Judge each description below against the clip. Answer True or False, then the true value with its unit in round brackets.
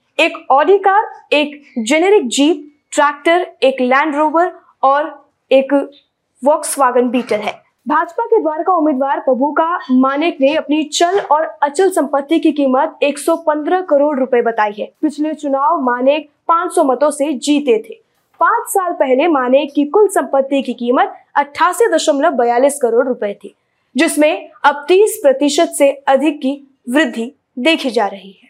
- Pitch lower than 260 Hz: False (295 Hz)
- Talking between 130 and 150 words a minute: True (140 wpm)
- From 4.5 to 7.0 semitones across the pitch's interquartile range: False (3.6 semitones)